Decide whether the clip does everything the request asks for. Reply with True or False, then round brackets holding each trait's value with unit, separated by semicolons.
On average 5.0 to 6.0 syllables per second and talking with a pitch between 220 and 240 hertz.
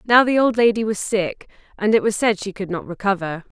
False (5.5 syllables/s; 205 Hz)